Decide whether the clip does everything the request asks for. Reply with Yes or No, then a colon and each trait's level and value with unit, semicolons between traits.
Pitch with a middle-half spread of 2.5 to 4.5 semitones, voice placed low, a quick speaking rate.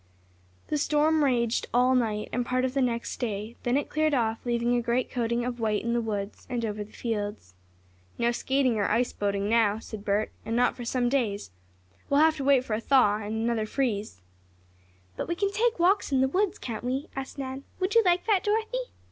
No: average, 3.9 semitones; high, 245 Hz; fast, 215 wpm